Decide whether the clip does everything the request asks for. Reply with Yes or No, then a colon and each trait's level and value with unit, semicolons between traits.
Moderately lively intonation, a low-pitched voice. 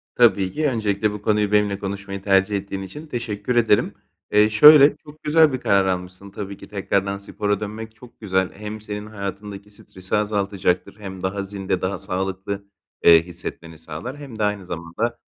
No: narrow, 2.0 semitones; low, 100 Hz